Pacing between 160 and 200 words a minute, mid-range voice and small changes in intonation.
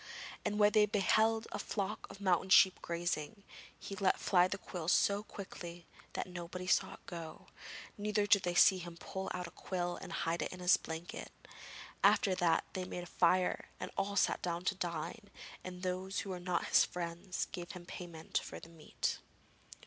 Yes: average, 185 wpm; medium, 180 Hz; narrow, 2.1 semitones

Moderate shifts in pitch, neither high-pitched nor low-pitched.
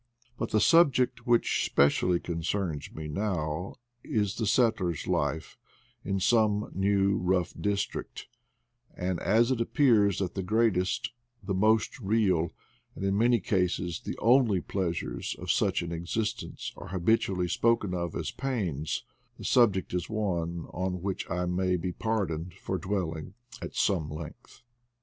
No: average, 4.0 semitones; very low, 95 Hz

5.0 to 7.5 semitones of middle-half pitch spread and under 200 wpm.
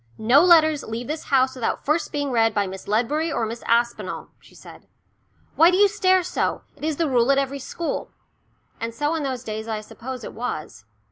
No: average, 5.3 semitones; fast, 205 wpm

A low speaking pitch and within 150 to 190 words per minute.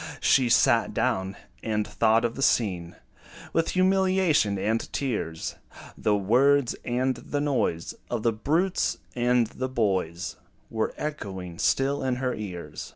No: low, 120 Hz; slow, 135 wpm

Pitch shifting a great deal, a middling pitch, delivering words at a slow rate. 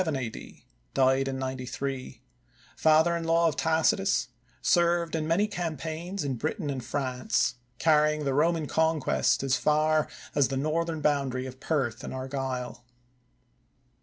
No: average, 3.5 semitones; medium, 150 Hz; slow, 125 wpm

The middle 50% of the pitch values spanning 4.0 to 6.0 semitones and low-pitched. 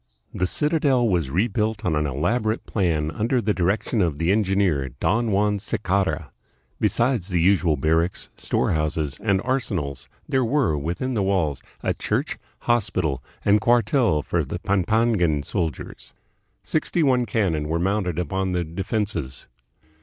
Yes: wide, 5.4 semitones; very low, 95 Hz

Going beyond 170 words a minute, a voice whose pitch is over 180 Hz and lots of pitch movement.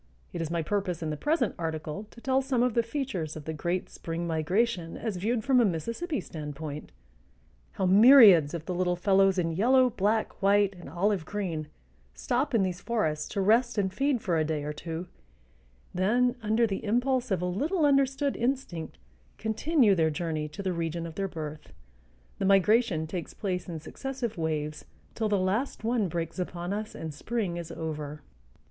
Yes: average, 180 wpm; high, 190 Hz; wide, 6.1 semitones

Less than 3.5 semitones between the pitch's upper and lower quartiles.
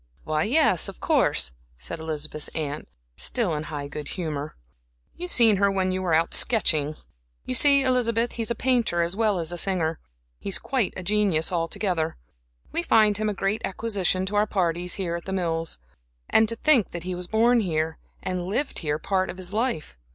No: average, 5.2 semitones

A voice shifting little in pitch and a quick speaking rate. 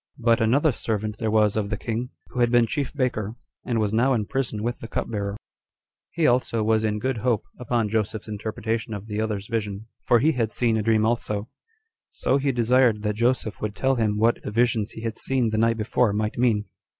Yes: narrow, 2.2 semitones; fast, 220 wpm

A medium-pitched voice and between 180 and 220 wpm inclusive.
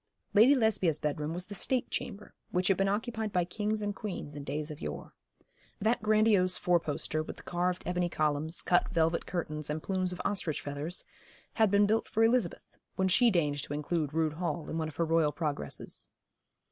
Yes: medium, 175 Hz; average, 195 wpm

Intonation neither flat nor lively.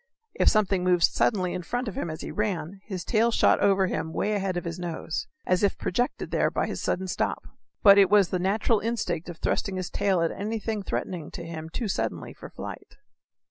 Yes: average, 3.1 semitones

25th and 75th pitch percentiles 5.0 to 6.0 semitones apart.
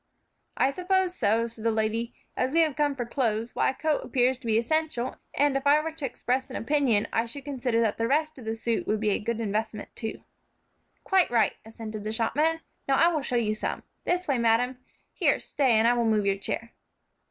No: average, 4.3 semitones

